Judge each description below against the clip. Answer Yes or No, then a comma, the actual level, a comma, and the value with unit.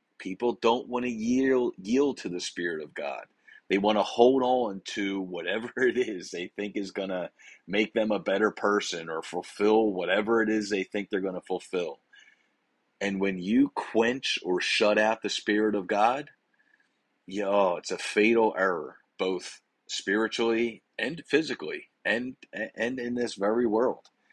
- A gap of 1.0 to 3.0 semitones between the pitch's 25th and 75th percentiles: No, average, 3.6 semitones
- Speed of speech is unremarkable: Yes, average, 165 wpm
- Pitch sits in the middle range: No, low, 110 Hz